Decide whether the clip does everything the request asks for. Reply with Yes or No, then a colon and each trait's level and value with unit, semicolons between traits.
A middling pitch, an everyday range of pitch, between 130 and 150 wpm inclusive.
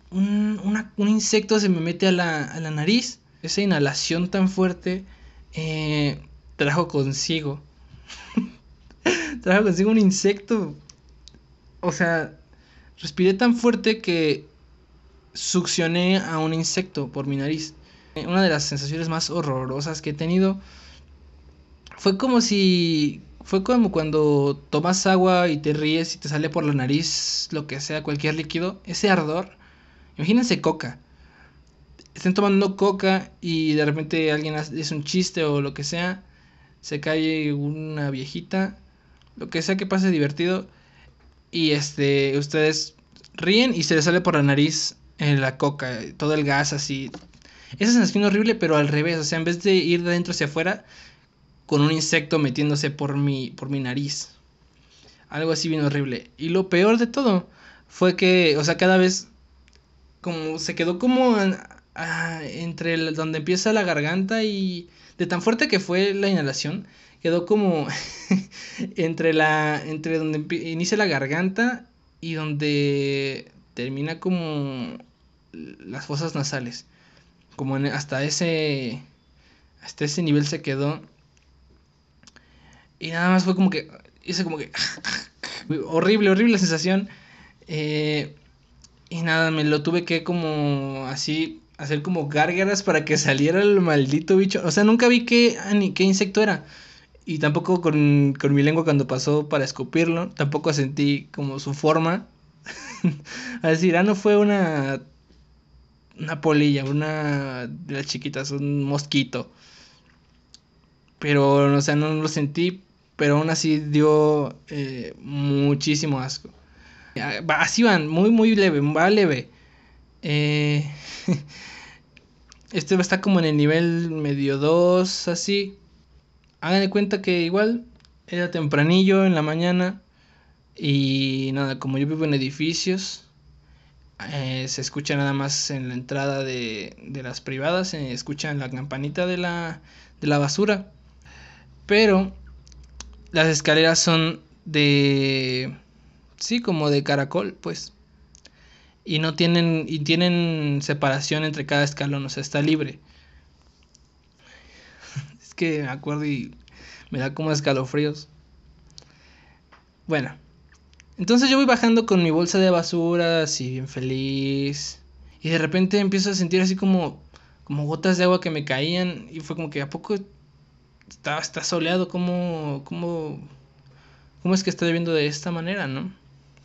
Yes: medium, 155 Hz; average, 4.6 semitones; average, 140 wpm